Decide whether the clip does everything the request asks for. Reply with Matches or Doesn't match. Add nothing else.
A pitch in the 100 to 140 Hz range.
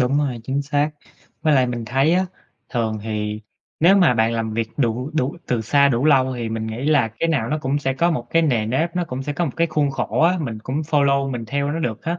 Matches